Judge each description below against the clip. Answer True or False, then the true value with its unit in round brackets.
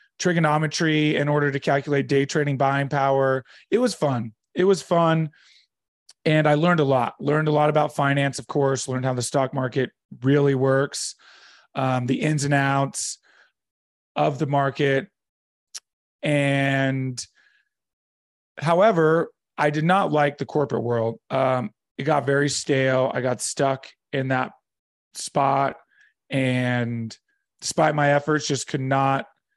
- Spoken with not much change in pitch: True (2.3 semitones)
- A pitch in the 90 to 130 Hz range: False (140 Hz)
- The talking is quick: False (140 wpm)